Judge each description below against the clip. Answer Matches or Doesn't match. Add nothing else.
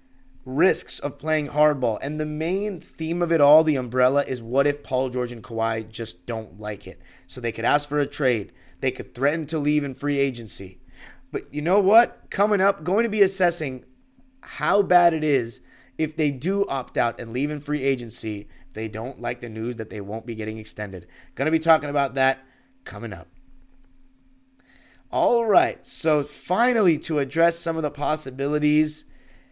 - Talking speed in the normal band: Matches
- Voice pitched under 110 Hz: Doesn't match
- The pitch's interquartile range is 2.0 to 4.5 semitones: Doesn't match